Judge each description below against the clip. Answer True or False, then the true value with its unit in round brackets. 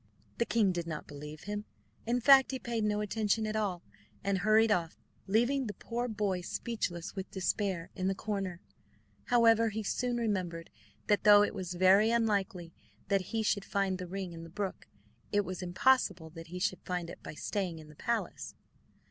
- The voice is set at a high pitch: True (200 Hz)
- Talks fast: False (185 wpm)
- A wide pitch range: False (3.6 semitones)